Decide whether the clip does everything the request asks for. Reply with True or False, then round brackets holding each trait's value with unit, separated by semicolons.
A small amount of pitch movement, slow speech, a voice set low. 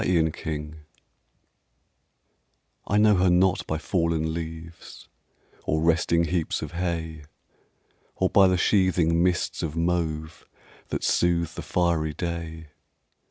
True (1.8 semitones; 115 wpm; 85 Hz)